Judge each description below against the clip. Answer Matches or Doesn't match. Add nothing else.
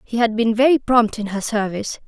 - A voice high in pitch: Matches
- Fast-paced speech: Matches